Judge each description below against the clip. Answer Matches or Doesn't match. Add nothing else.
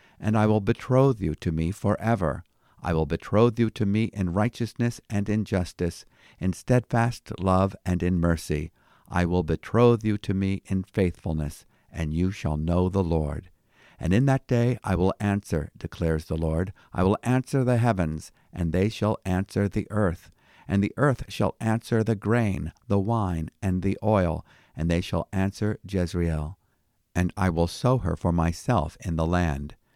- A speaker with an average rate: Matches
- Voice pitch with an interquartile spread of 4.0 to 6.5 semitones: Matches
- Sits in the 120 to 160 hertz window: Doesn't match